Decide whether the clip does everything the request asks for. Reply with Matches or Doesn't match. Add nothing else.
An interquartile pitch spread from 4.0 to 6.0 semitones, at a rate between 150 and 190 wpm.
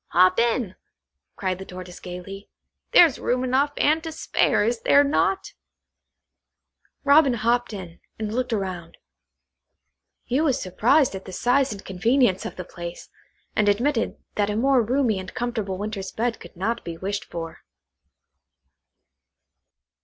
Doesn't match